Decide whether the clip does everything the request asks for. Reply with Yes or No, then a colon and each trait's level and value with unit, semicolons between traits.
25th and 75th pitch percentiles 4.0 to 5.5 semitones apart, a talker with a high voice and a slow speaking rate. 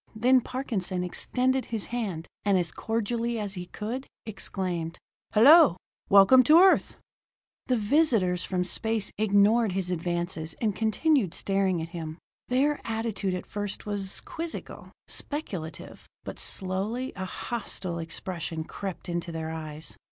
Yes: average, 4.8 semitones; high, 200 Hz; slow, 130 wpm